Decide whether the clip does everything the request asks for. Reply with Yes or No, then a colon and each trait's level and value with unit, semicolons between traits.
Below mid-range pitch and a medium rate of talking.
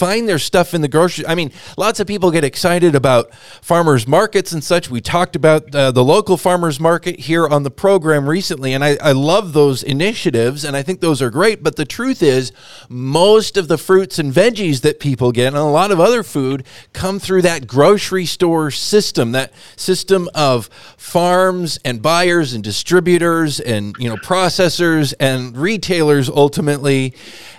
No: medium, 160 Hz; average, 180 wpm